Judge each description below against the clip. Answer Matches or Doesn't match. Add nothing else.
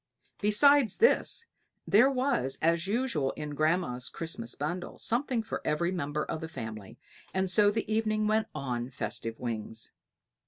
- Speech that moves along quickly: Doesn't match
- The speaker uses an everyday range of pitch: Doesn't match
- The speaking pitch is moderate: Matches